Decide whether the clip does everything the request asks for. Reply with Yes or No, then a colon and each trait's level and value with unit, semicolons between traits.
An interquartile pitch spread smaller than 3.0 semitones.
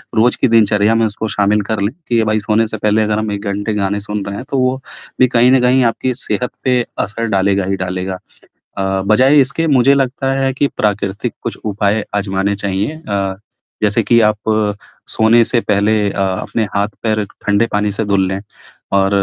Yes: narrow, 2.6 semitones